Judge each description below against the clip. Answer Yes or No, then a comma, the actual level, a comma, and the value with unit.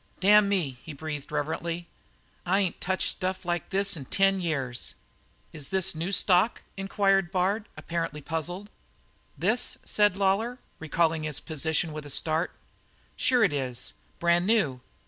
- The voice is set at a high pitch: No, medium, 175 Hz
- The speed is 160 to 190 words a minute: No, average, 145 wpm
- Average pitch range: Yes, average, 3.9 semitones